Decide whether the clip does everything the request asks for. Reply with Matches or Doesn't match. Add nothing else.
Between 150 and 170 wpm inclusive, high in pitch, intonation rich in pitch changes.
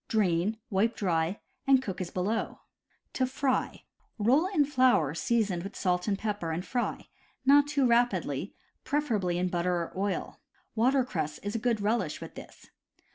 Matches